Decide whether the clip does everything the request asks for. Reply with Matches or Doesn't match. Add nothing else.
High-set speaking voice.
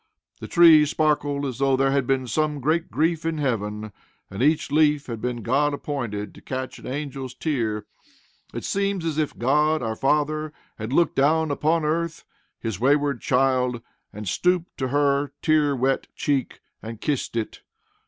Doesn't match